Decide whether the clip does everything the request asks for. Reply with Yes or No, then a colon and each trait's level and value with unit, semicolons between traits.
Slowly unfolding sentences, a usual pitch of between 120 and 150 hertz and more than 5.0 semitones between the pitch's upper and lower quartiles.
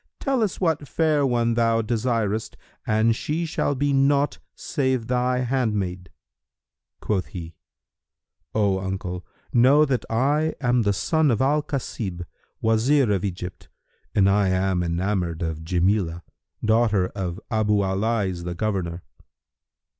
No: slow, 130 wpm; low, 110 Hz; wide, 5.6 semitones